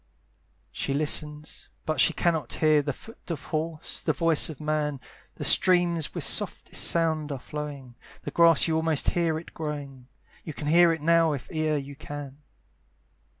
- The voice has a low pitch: No, medium, 155 Hz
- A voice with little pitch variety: Yes, narrow, 2.0 semitones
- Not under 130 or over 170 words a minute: Yes, average, 160 wpm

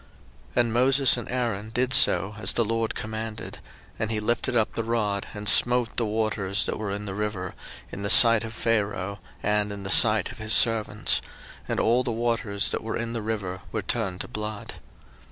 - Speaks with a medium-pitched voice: No, low, 110 Hz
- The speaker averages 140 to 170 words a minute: No, average, 200 wpm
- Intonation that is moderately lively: No, narrow, 2.1 semitones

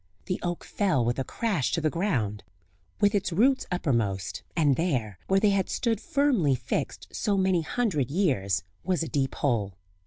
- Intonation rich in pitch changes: Yes, wide, 7.9 semitones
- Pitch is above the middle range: No, medium, 165 Hz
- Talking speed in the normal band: Yes, average, 175 wpm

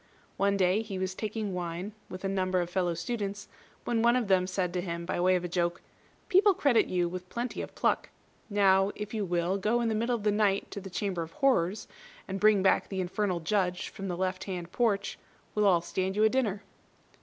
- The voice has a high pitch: Yes, high, 195 Hz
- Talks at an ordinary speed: No, fast, 225 wpm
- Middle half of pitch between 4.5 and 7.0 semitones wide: No, average, 2.7 semitones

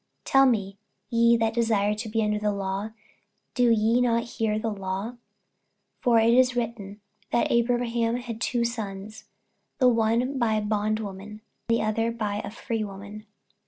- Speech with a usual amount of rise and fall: No, narrow, 2.0 semitones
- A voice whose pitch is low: No, high, 225 Hz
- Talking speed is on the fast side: No, average, 160 wpm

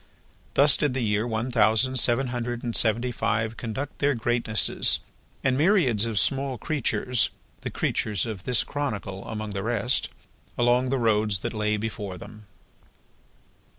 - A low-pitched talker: Yes, low, 115 Hz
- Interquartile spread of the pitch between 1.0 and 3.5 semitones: Yes, average, 3.0 semitones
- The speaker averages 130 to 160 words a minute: Yes, average, 150 wpm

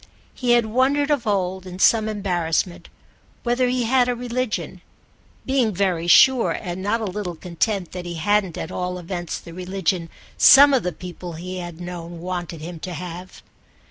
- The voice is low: No, medium, 185 Hz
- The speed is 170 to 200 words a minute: Yes, average, 175 wpm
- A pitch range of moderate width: Yes, average, 4.8 semitones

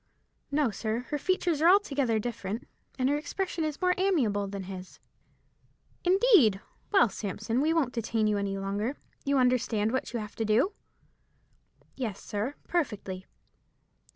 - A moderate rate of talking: Yes, average, 145 wpm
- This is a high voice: Yes, high, 245 Hz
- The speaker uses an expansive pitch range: Yes, wide, 6.6 semitones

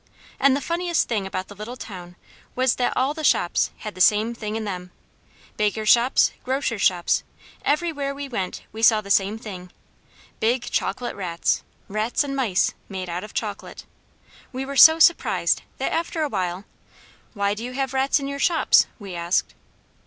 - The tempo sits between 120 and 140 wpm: No, average, 175 wpm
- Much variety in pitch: Yes, wide, 5.9 semitones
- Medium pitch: No, high, 225 Hz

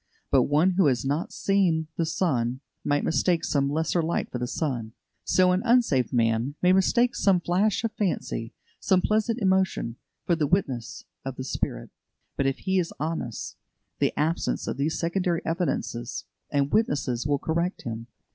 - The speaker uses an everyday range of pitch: No, wide, 5.7 semitones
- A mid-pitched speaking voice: Yes, medium, 160 Hz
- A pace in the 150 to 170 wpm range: Yes, average, 165 wpm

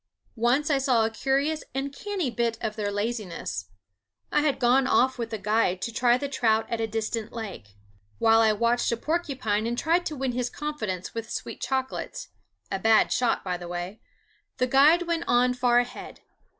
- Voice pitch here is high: Yes, high, 240 Hz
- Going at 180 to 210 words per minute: Yes, average, 190 wpm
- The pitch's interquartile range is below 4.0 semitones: Yes, average, 3.6 semitones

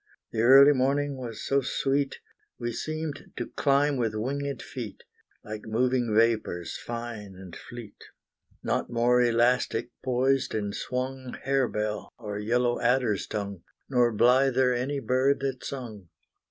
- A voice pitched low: Yes, low, 125 Hz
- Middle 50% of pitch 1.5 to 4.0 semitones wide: Yes, average, 3.3 semitones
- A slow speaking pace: Yes, slow, 130 wpm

